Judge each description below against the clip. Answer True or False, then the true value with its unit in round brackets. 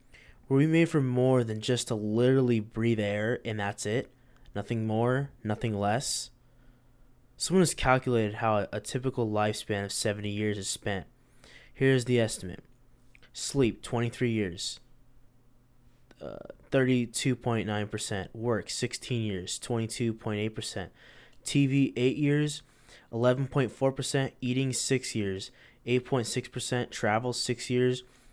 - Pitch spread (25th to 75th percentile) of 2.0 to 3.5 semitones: True (2.5 semitones)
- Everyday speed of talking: False (110 wpm)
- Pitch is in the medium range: False (120 Hz)